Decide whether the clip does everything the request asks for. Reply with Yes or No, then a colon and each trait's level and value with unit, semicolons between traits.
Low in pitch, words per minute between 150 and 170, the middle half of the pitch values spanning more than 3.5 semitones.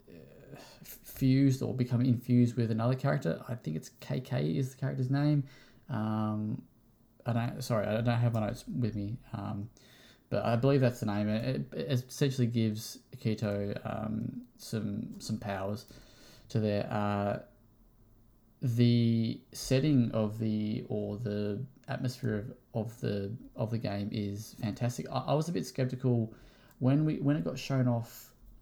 No: low, 115 Hz; average, 155 wpm; average, 2.7 semitones